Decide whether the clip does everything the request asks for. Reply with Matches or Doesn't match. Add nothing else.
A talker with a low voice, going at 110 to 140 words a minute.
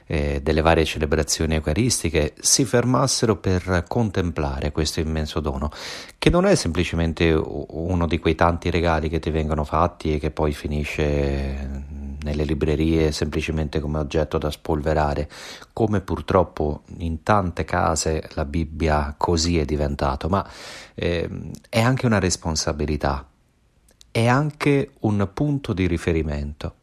Matches